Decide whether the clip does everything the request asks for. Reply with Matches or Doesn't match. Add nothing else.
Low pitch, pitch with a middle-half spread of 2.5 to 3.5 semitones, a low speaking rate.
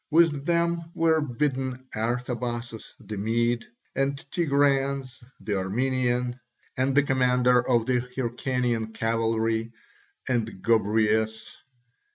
Matches